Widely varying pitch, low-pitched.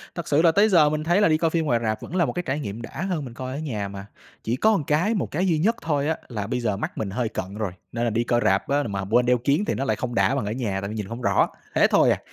Yes: wide, 6.4 semitones; low, 130 Hz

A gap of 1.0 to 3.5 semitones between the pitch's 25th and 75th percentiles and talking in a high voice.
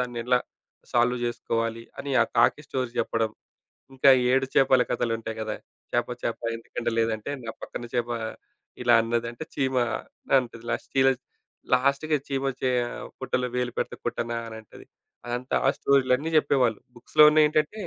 No: narrow, 2.4 semitones; low, 125 Hz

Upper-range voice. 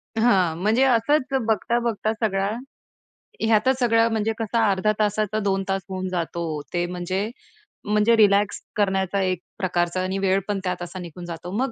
Yes: high, 200 Hz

